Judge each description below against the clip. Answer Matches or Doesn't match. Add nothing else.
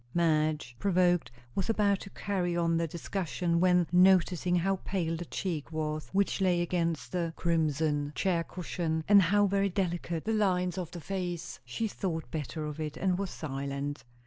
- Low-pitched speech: Doesn't match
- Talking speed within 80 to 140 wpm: Doesn't match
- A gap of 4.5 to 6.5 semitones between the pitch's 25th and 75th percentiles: Doesn't match